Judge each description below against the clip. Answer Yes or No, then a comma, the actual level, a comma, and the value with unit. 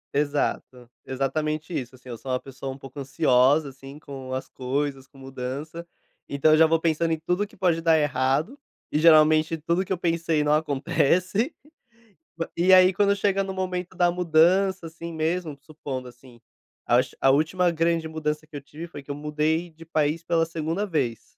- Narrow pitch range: No, average, 3.7 semitones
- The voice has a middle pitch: Yes, medium, 155 Hz